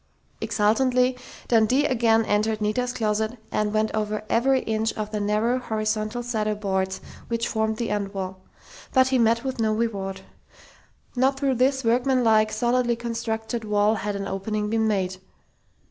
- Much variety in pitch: No, narrow, 2.5 semitones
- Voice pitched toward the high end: Yes, high, 220 Hz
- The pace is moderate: Yes, average, 150 wpm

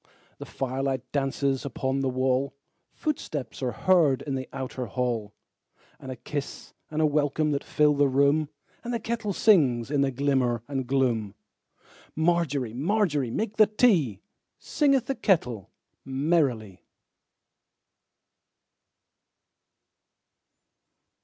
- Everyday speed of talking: No, slow, 100 wpm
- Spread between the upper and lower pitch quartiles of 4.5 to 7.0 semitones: No, average, 3.7 semitones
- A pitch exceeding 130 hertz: Yes, medium, 140 Hz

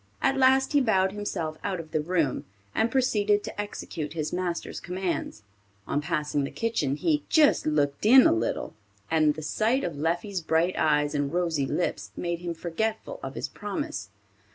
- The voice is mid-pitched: Yes, medium, 175 Hz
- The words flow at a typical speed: Yes, average, 175 wpm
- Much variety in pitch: Yes, wide, 5.8 semitones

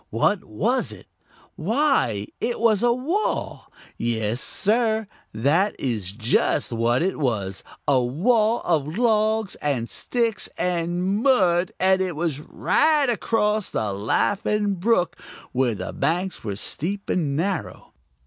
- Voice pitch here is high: No, medium, 180 Hz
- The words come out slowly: Yes, slow, 130 wpm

